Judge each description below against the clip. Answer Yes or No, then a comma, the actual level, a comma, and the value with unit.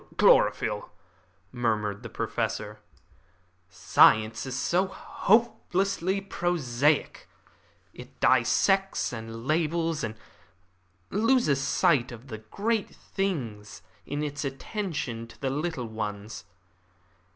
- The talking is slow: Yes, slow, 95 wpm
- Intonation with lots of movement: Yes, wide, 8.4 semitones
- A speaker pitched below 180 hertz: Yes, medium, 140 Hz